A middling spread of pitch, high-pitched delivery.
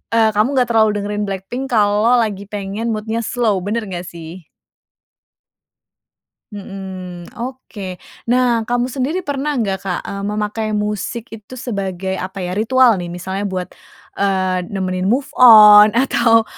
Yes: average, 3.6 semitones; high, 210 Hz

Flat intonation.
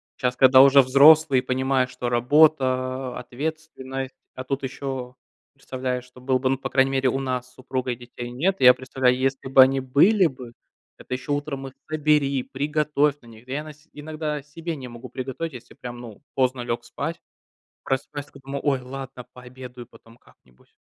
Yes: narrow, 2.0 semitones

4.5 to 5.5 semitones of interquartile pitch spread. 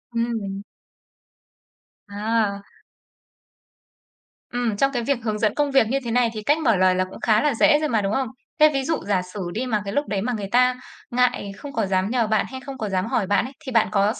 No: average, 3.8 semitones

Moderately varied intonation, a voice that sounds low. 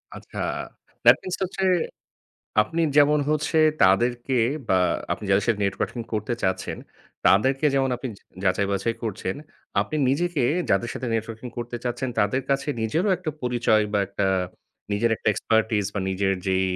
Yes: average, 4.9 semitones; low, 115 Hz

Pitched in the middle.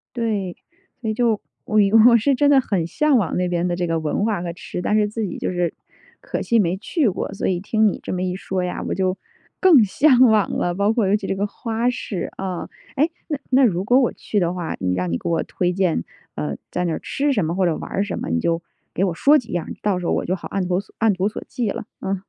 No: high, 195 Hz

